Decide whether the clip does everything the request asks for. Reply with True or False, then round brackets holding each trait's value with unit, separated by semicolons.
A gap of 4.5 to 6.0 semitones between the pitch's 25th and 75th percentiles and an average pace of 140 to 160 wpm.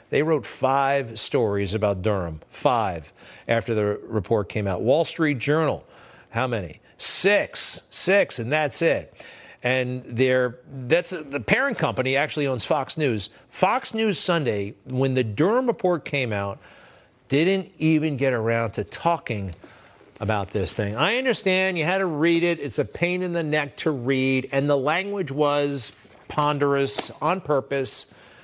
True (5.4 semitones; 150 wpm)